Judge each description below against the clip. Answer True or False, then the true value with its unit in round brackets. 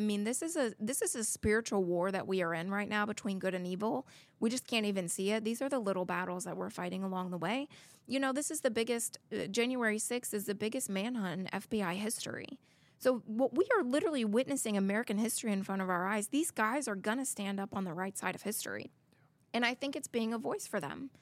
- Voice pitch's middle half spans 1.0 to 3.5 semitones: False (4.1 semitones)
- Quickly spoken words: True (245 wpm)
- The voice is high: True (215 Hz)